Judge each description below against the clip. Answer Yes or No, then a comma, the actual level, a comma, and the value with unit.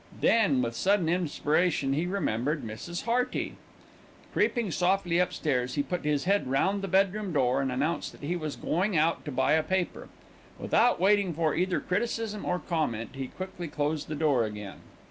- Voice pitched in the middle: Yes, medium, 165 Hz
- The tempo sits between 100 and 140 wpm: No, average, 170 wpm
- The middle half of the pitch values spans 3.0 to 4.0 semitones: No, average, 5.2 semitones